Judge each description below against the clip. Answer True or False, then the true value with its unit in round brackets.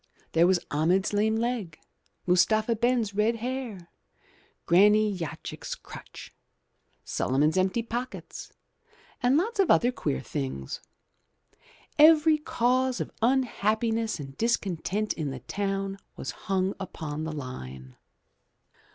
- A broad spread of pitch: True (6.1 semitones)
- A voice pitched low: False (205 Hz)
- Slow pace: True (110 wpm)